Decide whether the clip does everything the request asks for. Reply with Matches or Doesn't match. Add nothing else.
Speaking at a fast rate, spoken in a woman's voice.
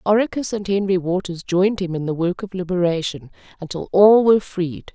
Doesn't match